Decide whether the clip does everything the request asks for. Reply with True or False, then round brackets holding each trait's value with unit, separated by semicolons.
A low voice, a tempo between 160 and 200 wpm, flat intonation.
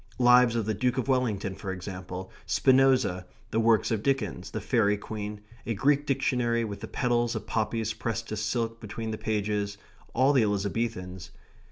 False (110 Hz; 170 wpm; 3.0 semitones)